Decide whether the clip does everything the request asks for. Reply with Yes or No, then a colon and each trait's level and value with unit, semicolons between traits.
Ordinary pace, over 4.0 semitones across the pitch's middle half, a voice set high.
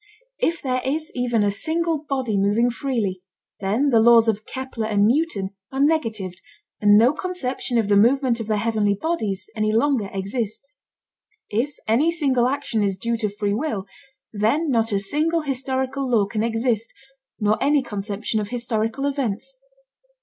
Yes: average, 160 wpm; average, 4.6 semitones; high, 230 Hz